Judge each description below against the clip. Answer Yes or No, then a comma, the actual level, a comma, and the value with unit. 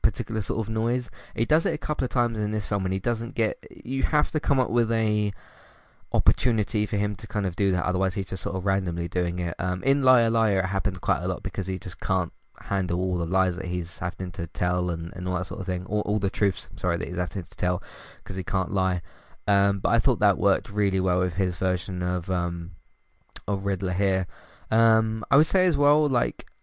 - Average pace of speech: No, fast, 240 wpm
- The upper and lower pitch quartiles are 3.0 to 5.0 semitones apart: Yes, average, 3.3 semitones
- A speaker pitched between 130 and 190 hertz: No, very low, 95 Hz